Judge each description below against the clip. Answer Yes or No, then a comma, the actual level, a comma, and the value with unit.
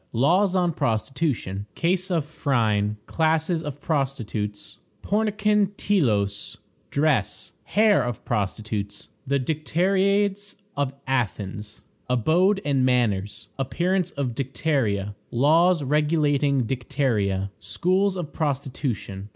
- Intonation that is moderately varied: No, wide, 7.8 semitones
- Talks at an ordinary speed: No, slow, 95 wpm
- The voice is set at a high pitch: No, medium, 140 Hz